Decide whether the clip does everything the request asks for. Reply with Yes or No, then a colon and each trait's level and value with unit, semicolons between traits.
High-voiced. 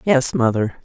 No: medium, 155 Hz